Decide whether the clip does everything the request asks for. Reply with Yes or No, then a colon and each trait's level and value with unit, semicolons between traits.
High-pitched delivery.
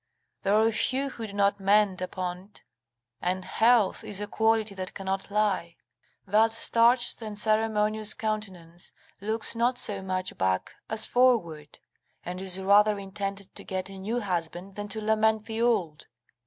Yes: high, 205 Hz